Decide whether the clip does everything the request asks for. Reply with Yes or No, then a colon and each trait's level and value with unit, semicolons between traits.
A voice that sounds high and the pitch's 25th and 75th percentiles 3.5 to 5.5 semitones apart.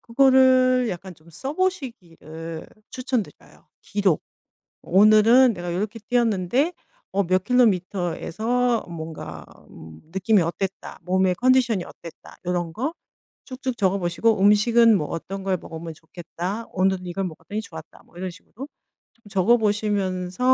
Yes: high, 195 Hz; average, 5.2 semitones